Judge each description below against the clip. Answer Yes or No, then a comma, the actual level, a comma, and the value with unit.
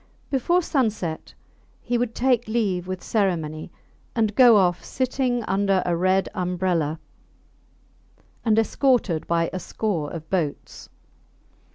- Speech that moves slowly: Yes, slow, 120 wpm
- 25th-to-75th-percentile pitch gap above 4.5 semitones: Yes, wide, 5.4 semitones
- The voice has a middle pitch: No, high, 195 Hz